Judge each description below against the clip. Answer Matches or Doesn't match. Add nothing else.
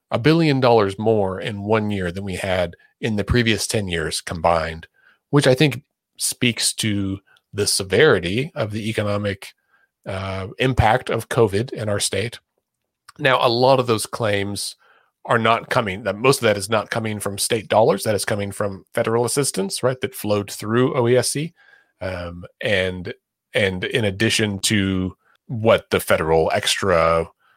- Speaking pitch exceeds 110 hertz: Doesn't match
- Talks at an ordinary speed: Matches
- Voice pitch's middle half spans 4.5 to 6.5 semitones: Doesn't match